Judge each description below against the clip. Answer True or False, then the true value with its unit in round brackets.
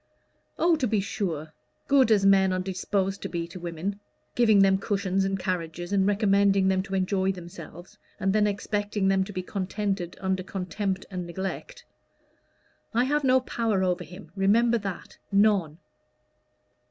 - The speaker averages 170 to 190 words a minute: False (155 wpm)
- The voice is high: True (195 Hz)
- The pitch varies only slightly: True (2.0 semitones)